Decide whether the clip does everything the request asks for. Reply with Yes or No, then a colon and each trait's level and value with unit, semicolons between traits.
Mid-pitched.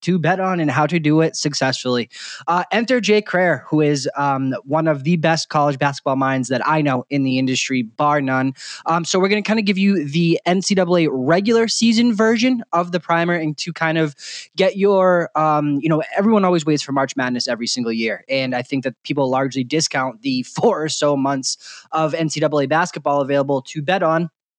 Yes: medium, 155 Hz